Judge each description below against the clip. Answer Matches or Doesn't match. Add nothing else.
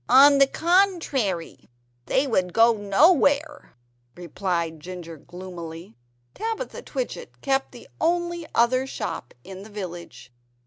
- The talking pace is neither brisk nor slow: Doesn't match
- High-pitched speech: Matches